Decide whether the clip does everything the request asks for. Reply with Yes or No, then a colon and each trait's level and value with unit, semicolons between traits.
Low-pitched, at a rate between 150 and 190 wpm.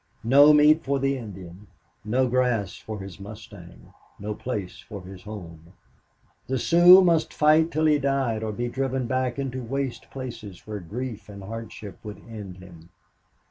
Yes: low, 115 Hz; average, 160 wpm